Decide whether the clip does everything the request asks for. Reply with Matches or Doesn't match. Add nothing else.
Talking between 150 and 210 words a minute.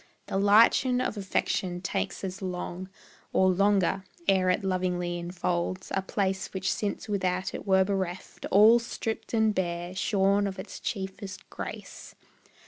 Doesn't match